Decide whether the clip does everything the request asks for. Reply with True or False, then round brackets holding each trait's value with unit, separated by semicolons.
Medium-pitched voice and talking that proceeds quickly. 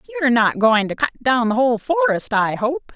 False (225 Hz; 225 wpm)